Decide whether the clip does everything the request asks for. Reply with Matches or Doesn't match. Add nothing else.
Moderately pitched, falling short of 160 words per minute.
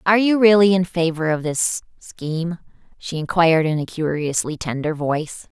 Matches